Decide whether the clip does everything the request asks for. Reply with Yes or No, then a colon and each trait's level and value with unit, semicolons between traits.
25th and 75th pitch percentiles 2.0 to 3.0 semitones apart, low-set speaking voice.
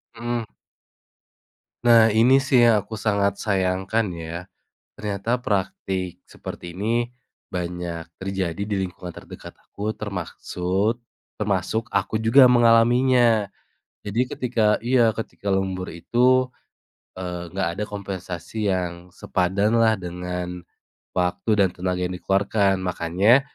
No: average, 3.8 semitones; low, 100 Hz